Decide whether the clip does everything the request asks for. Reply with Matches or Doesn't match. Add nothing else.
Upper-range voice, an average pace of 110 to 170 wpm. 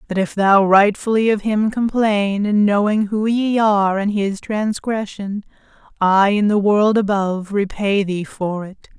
Matches